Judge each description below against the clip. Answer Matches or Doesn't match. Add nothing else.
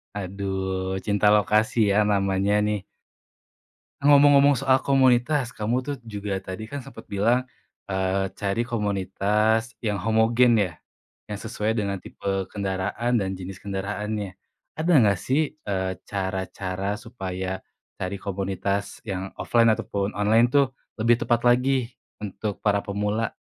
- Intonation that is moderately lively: Matches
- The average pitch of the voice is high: Doesn't match